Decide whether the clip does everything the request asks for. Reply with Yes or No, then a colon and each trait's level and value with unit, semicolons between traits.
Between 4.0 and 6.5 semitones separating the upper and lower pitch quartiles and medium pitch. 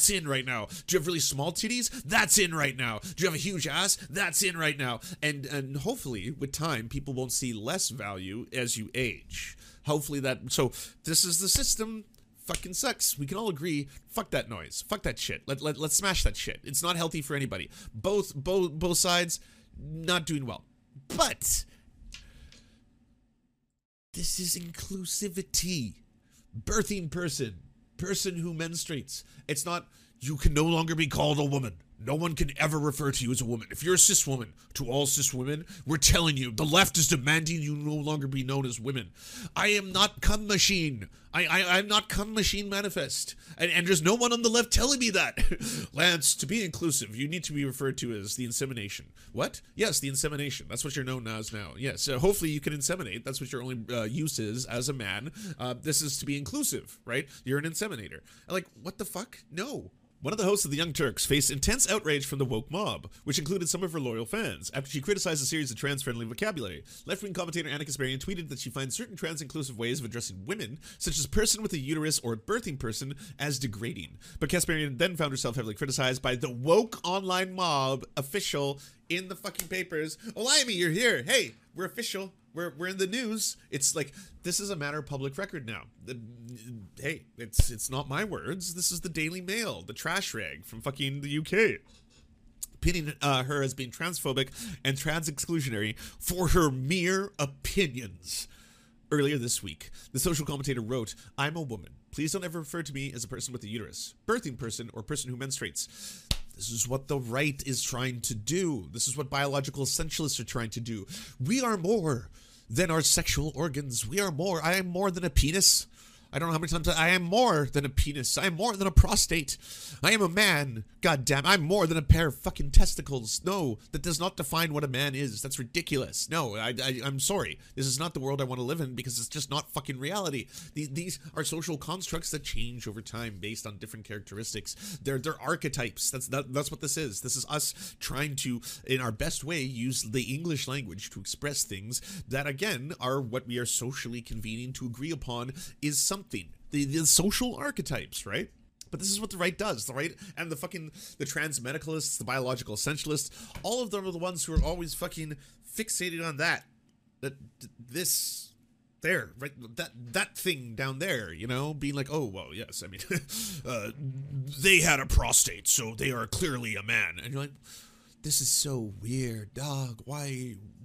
Yes: wide, 5.6 semitones; medium, 145 Hz